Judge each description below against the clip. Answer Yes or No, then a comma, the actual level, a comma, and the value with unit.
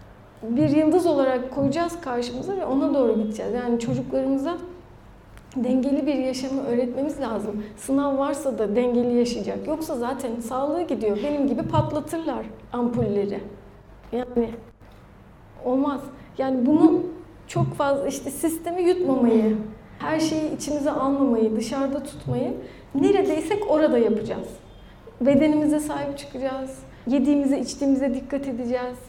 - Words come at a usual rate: Yes, average, 110 wpm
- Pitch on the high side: Yes, very high, 270 Hz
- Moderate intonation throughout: Yes, average, 3.3 semitones